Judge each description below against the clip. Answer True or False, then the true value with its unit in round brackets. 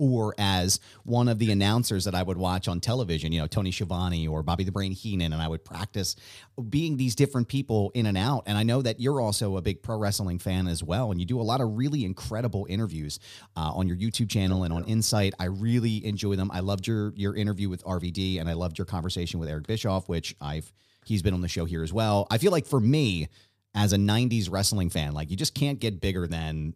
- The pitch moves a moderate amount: True (3.8 semitones)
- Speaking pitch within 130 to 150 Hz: False (100 Hz)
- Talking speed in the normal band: False (240 wpm)